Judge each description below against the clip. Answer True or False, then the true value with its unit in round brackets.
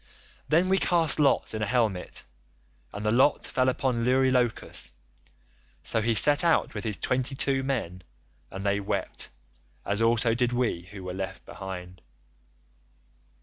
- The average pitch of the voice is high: False (115 Hz)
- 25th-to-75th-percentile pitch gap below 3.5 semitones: False (4.7 semitones)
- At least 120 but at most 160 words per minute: True (145 wpm)